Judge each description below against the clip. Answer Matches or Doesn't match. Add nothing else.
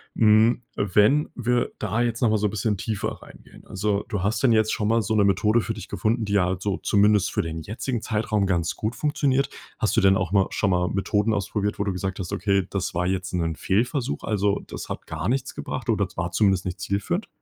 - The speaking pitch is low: Matches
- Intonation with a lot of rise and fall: Doesn't match